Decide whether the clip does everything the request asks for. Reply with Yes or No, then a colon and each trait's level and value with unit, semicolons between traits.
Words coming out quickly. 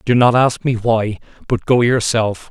No: average, 190 wpm